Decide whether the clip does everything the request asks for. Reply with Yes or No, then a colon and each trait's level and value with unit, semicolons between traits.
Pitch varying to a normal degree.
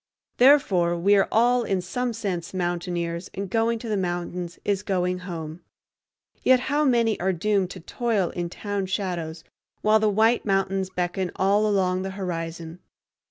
Yes: average, 3.3 semitones